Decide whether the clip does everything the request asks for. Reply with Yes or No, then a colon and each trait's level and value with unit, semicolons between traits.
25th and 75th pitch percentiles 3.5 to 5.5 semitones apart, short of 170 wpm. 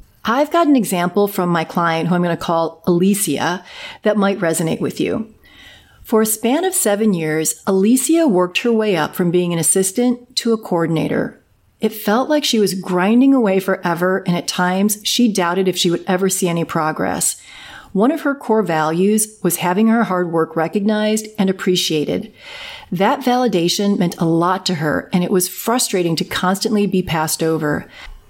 No: average, 4.0 semitones; average, 180 wpm